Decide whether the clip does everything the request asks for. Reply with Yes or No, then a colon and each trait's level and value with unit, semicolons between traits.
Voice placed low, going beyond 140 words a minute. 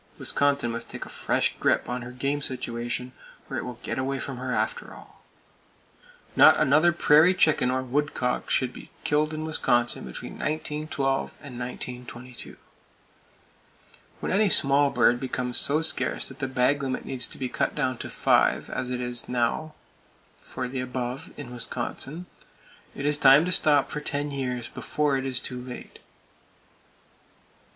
Yes: low, 130 Hz; average, 160 wpm